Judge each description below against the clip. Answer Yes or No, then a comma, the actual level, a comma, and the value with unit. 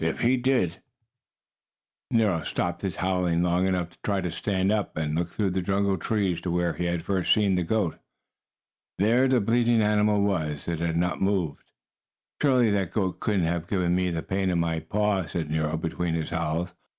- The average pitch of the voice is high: No, very low, 90 Hz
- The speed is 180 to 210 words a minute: Yes, average, 195 wpm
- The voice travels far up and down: No, average, 3.2 semitones